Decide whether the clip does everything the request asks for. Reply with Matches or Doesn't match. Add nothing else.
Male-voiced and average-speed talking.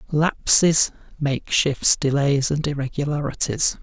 Doesn't match